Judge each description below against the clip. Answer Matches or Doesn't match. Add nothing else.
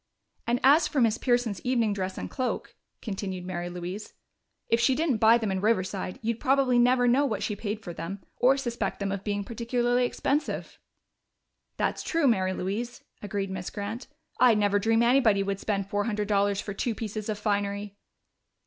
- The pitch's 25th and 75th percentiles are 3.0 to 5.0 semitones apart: Matches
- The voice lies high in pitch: Matches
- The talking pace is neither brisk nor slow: Matches